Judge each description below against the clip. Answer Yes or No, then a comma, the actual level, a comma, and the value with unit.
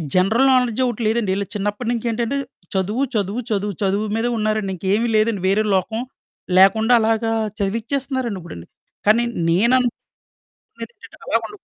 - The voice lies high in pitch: Yes, high, 220 Hz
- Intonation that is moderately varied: Yes, average, 3.1 semitones